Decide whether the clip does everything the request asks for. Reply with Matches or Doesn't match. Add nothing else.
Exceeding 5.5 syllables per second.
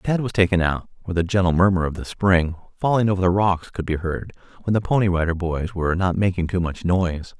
Matches